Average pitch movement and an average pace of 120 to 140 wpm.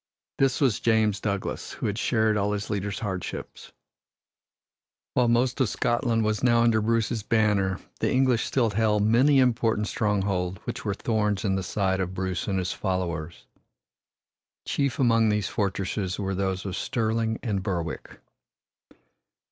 No: average, 3.2 semitones; average, 150 wpm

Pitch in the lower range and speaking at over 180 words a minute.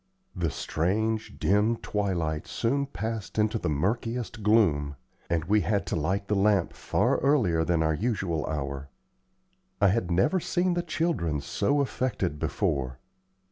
No: low, 100 Hz; average, 140 wpm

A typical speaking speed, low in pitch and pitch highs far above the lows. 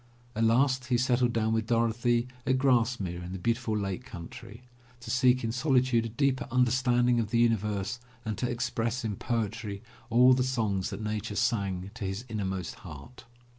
No: average, 170 wpm; low, 115 Hz; average, 2.8 semitones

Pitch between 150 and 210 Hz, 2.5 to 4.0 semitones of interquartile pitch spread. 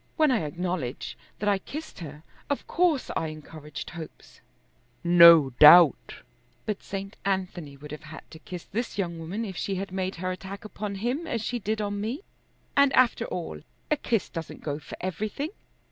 No: high, 190 Hz; average, 5.0 semitones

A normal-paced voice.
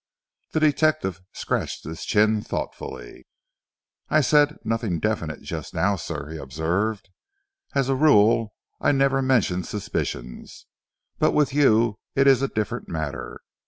No: slow, 130 wpm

